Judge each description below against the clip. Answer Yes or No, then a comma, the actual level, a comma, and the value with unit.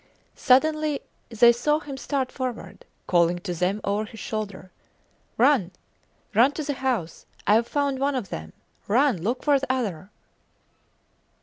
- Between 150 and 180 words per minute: No, average, 140 wpm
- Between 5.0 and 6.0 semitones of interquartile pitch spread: Yes, wide, 5.6 semitones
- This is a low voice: No, high, 245 Hz